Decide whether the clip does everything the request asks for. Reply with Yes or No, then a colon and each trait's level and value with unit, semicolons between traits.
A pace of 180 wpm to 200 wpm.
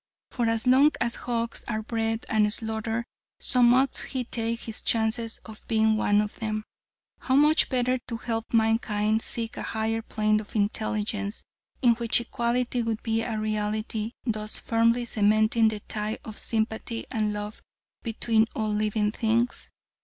No: average, 155 wpm